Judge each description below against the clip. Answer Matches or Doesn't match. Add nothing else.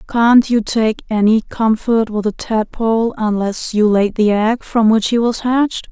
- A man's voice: Doesn't match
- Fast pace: Doesn't match